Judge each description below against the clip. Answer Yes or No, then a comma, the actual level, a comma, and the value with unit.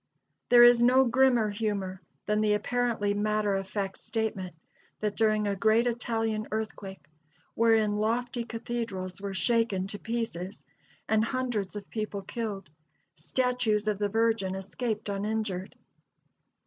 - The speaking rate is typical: No, slow, 130 wpm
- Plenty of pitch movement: No, narrow, 2.5 semitones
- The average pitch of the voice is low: No, high, 215 Hz